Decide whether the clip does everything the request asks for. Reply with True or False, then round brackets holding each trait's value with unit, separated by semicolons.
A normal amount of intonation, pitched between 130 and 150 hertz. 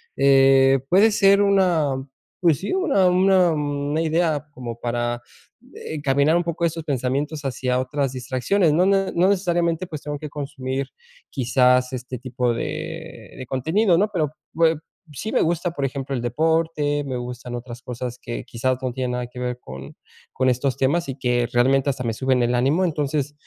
True (4.6 semitones; 140 Hz)